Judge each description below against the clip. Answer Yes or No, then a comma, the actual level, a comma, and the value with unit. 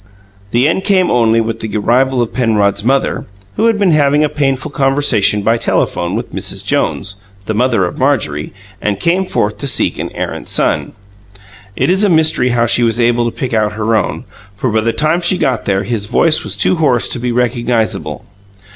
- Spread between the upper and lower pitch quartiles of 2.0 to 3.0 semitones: No, average, 4.7 semitones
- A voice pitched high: No, low, 120 Hz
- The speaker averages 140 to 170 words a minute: No, average, 200 wpm